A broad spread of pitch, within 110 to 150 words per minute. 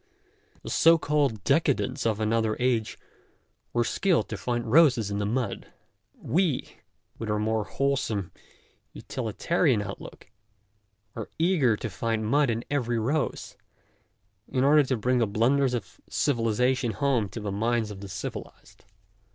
No: average, 4.2 semitones; average, 140 wpm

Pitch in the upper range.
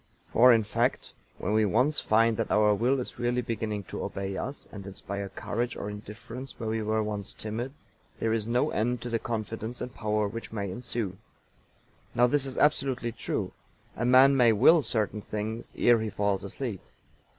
No: low, 115 Hz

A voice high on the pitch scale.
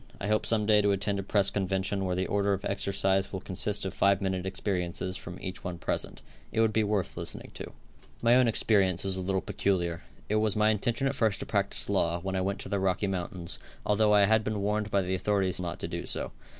No: low, 100 Hz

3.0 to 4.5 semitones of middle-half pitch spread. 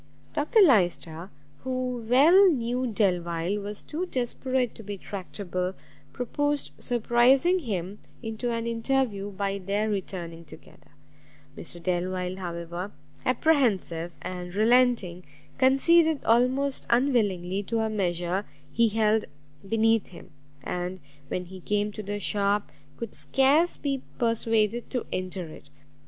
No: average, 5.3 semitones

